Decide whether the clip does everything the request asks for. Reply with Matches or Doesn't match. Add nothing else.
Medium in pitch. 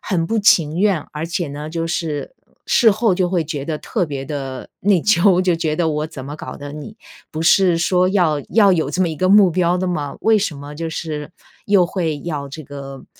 Matches